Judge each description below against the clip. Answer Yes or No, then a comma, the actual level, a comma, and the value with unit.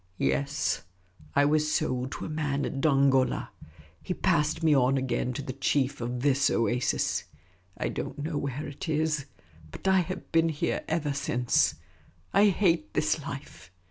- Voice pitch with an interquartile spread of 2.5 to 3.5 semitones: Yes, average, 3.1 semitones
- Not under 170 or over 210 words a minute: No, average, 160 wpm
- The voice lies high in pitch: No, medium, 145 Hz